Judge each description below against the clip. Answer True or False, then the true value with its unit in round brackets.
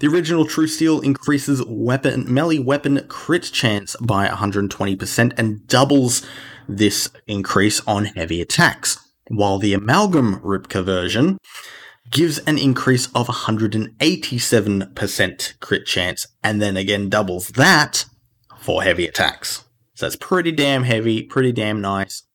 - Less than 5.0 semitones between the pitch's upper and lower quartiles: False (5.4 semitones)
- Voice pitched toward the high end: False (120 Hz)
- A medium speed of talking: False (125 wpm)